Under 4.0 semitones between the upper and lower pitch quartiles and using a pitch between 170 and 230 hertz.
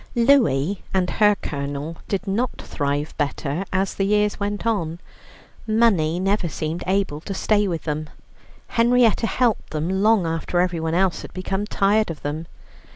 No: average, 4.6 semitones; high, 190 Hz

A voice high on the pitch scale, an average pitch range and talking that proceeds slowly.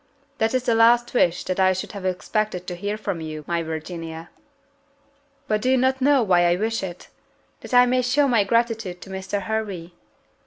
No: high, 205 Hz; average, 5.0 semitones; average, 195 wpm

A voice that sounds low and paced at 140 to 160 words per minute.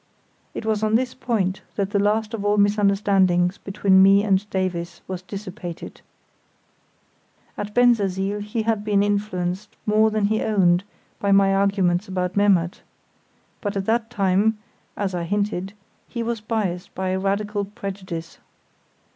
No: high, 200 Hz; average, 145 wpm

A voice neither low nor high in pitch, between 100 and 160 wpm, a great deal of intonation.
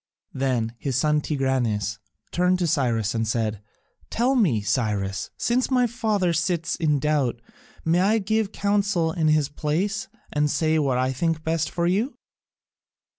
Yes: medium, 155 Hz; average, 150 wpm; wide, 6.3 semitones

